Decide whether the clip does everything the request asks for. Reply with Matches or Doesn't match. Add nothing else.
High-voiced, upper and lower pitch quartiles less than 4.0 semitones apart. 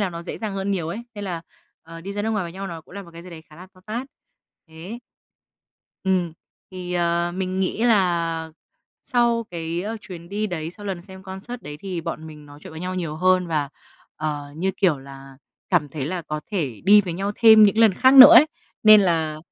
Doesn't match